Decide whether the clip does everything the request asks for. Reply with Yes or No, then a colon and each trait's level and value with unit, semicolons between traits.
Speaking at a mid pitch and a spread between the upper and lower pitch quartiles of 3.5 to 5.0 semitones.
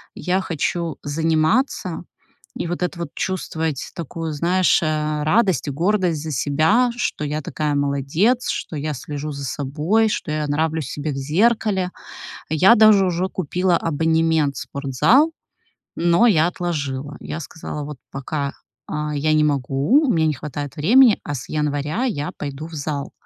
Yes: medium, 155 Hz; average, 3.9 semitones